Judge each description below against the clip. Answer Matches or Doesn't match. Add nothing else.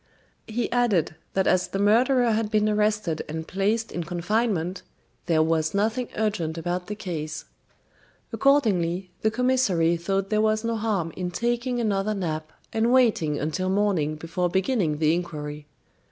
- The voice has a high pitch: Matches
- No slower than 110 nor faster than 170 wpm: Matches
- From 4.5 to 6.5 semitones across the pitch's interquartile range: Matches